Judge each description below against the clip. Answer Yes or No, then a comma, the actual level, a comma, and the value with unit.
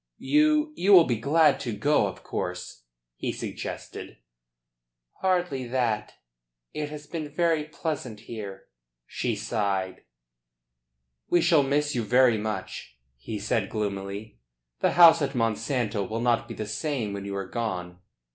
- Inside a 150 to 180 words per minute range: No, average, 140 wpm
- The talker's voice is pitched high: No, low, 120 Hz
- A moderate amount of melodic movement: No, wide, 6.4 semitones